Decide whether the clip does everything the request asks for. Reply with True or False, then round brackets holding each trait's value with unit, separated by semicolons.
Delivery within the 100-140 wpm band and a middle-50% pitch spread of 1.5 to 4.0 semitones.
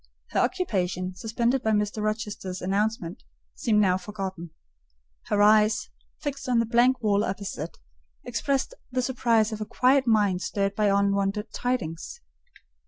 True (135 wpm; 3.1 semitones)